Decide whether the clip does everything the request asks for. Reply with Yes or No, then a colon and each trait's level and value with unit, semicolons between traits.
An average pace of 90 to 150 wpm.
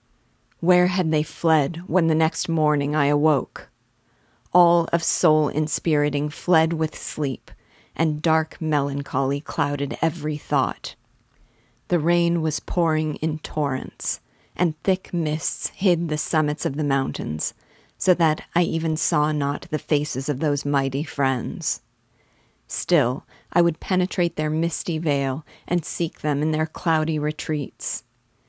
Yes: slow, 135 wpm